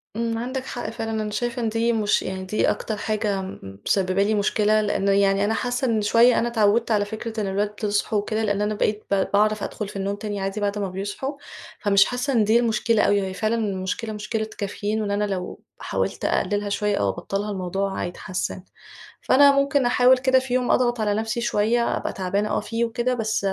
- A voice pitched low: No, high, 215 Hz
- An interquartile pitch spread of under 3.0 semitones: Yes, narrow, 2.4 semitones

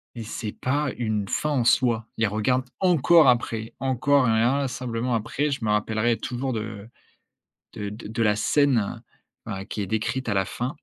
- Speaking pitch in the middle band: No, low, 115 Hz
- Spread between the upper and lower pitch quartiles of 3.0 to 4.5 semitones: Yes, average, 3.3 semitones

